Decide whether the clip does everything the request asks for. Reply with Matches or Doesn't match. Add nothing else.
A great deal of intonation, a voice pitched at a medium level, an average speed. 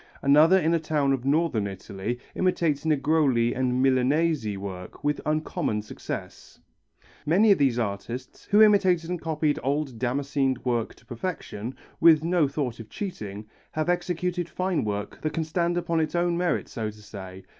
Matches